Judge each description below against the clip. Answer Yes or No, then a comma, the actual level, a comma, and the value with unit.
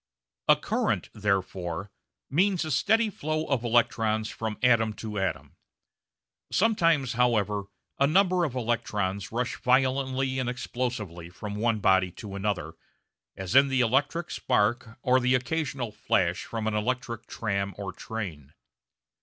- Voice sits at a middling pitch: No, low, 115 Hz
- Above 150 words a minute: No, slow, 135 wpm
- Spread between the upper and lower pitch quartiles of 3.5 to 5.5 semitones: Yes, average, 4.3 semitones